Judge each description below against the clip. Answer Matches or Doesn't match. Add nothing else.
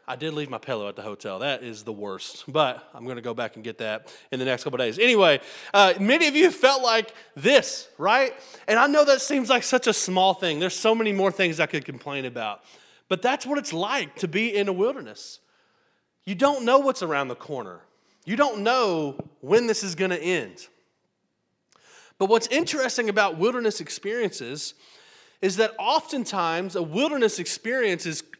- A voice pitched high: Matches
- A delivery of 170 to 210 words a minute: Matches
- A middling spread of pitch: Doesn't match